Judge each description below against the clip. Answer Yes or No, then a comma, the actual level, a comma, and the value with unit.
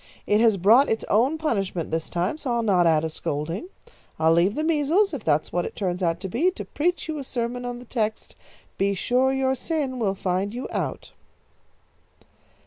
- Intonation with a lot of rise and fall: Yes, wide, 6.7 semitones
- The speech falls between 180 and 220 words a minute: Yes, average, 200 wpm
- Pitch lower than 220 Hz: No, high, 225 Hz